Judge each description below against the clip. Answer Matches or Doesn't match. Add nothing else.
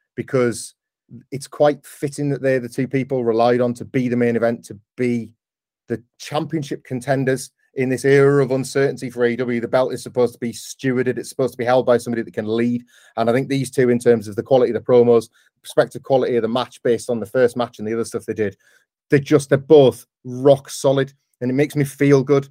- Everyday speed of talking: Doesn't match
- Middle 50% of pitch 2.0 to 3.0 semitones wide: Matches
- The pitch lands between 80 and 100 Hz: Doesn't match